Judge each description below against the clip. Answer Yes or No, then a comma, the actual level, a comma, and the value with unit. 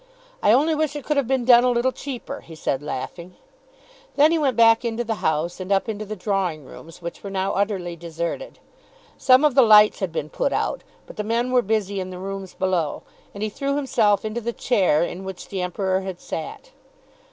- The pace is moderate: No, fast, 215 wpm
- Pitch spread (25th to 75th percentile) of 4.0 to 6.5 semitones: Yes, average, 5.1 semitones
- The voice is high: Yes, high, 205 Hz